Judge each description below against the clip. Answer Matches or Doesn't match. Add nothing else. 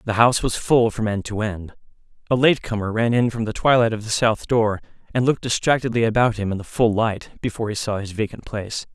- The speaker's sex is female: Doesn't match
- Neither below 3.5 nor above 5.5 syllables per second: Doesn't match